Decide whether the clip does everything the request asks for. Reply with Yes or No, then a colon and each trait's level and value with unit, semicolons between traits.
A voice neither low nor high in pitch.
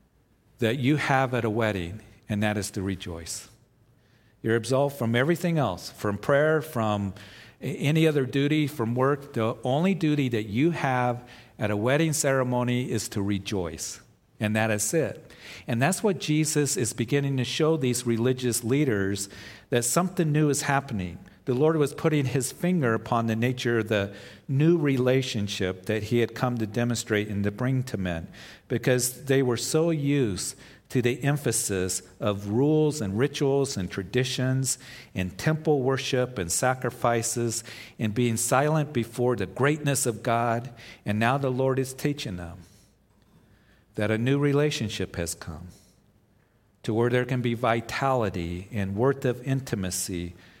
No: low, 120 Hz